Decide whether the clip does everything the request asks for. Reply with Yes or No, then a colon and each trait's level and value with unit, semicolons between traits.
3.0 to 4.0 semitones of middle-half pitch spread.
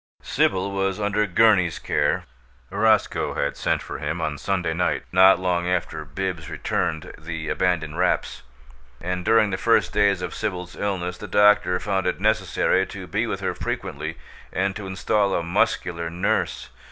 No: narrow, 2.6 semitones